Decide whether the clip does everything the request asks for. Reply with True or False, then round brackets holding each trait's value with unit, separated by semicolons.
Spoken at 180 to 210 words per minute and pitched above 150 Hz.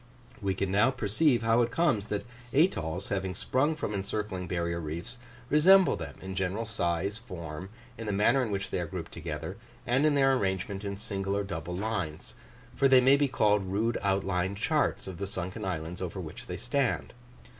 False (190 wpm; 100 Hz)